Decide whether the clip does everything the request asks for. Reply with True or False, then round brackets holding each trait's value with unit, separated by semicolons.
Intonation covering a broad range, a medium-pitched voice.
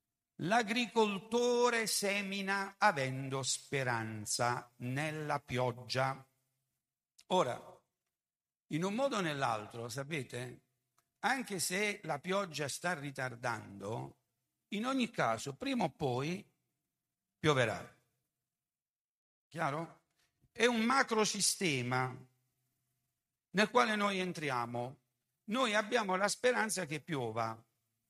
True (8.2 semitones; 145 Hz)